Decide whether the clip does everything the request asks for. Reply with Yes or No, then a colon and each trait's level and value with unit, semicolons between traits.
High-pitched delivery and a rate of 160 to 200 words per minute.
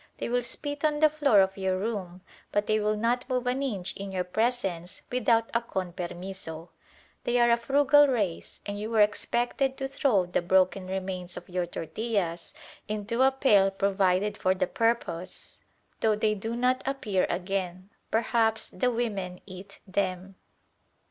Yes: high, 205 Hz; average, 165 wpm